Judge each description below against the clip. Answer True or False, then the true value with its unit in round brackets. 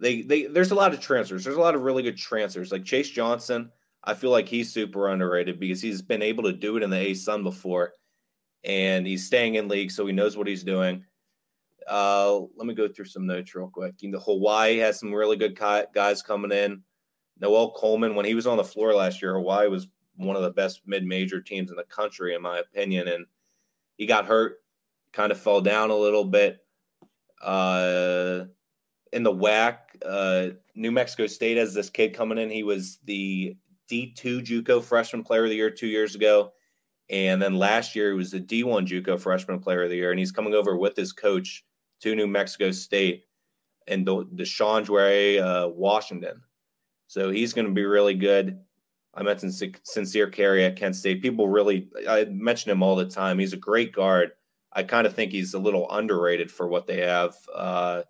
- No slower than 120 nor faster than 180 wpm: False (200 wpm)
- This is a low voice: True (100 Hz)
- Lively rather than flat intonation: False (2.9 semitones)